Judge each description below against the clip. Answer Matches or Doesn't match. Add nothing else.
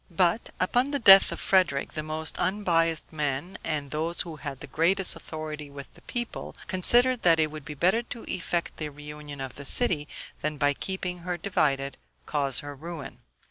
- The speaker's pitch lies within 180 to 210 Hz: Doesn't match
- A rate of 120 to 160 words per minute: Doesn't match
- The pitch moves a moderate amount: Matches